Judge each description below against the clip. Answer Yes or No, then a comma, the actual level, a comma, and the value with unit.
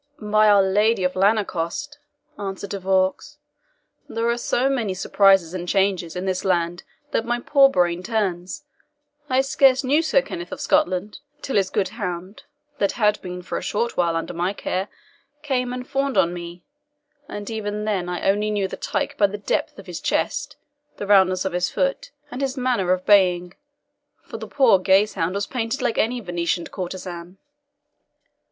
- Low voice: No, high, 200 Hz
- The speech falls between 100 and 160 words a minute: No, average, 175 wpm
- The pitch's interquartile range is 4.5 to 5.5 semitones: Yes, average, 4.8 semitones